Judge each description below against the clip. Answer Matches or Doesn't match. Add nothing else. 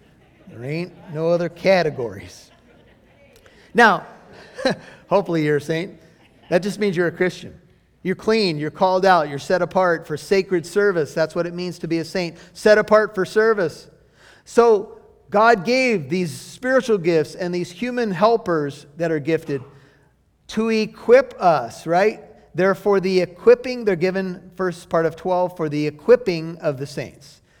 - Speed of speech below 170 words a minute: Matches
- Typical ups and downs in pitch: Matches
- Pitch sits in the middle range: Matches